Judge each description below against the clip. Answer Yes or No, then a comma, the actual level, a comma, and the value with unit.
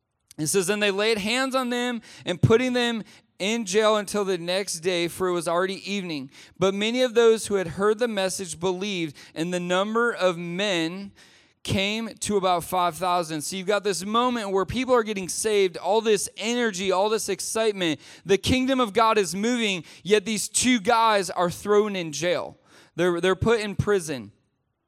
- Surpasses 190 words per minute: No, average, 185 wpm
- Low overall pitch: No, high, 195 Hz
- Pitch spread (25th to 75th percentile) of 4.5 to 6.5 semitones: No, average, 3.6 semitones